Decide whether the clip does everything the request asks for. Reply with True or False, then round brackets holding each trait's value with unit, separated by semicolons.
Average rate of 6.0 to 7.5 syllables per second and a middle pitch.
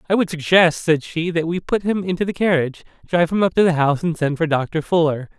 True (6.2 syllables/s; 165 Hz)